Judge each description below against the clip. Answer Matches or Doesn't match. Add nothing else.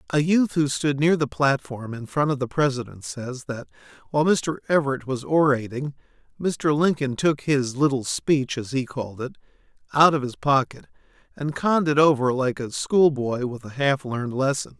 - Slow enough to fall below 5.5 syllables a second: Matches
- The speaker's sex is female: Doesn't match